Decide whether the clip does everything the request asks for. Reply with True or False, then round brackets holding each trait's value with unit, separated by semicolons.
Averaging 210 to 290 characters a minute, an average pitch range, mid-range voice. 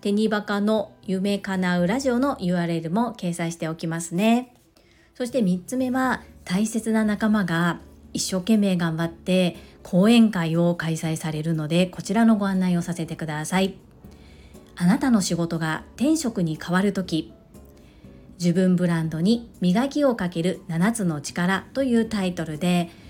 True (280 characters per minute; 4.5 semitones; 180 Hz)